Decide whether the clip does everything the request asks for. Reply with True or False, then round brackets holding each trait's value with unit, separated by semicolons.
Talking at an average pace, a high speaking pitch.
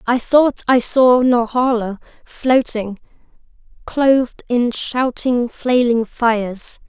False (95 wpm; 240 Hz)